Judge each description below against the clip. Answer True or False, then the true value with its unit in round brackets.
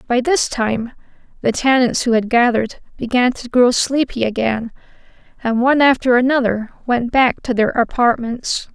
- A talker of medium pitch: False (245 Hz)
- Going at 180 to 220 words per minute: False (150 wpm)